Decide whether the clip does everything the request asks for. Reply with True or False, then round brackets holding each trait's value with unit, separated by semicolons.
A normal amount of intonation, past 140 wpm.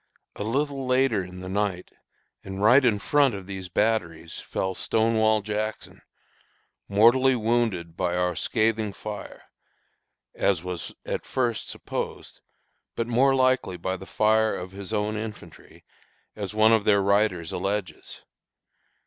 False (3.3 semitones; 135 wpm)